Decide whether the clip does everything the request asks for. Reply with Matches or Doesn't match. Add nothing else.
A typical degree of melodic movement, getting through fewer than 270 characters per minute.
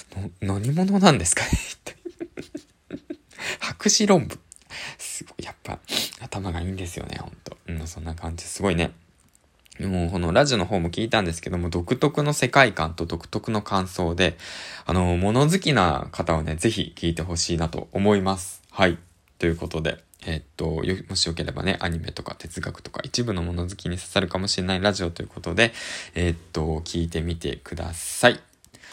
Doesn't match